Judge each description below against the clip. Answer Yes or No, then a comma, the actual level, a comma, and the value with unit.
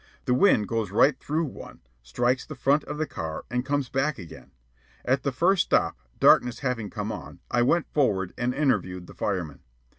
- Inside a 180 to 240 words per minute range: Yes, average, 185 wpm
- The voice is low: Yes, low, 125 Hz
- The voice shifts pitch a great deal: Yes, wide, 5.7 semitones